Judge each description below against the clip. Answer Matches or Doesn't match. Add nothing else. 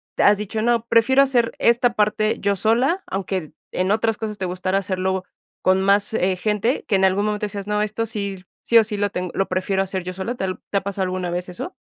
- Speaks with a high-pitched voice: Matches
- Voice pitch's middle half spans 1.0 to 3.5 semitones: Matches